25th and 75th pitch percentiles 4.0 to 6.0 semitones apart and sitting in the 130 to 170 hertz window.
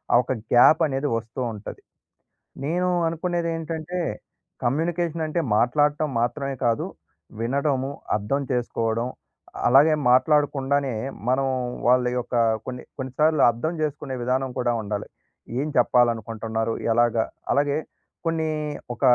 Yes: average, 4.3 semitones; low, 135 Hz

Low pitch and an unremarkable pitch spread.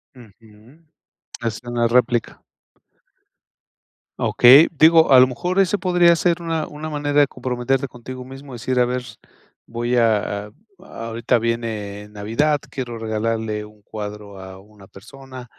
Yes: low, 120 Hz; average, 4.3 semitones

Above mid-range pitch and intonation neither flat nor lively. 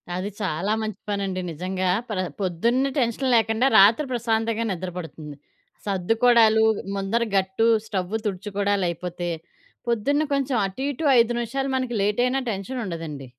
Yes: high, 210 Hz; average, 4.2 semitones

